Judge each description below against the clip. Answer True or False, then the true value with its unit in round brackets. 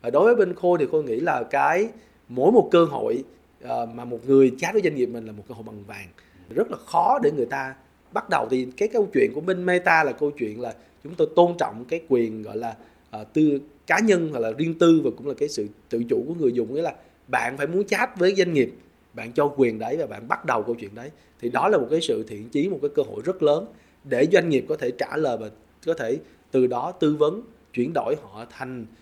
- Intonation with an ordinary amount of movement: False (8.1 semitones)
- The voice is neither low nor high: True (150 Hz)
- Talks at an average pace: False (260 wpm)